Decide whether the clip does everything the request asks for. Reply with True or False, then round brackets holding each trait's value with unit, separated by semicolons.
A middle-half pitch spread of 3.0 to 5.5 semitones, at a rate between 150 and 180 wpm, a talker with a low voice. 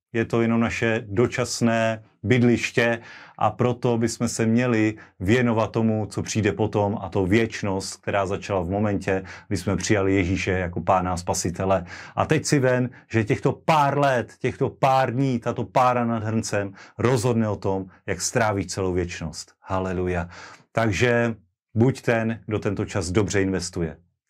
True (3.6 semitones; 155 wpm; 110 Hz)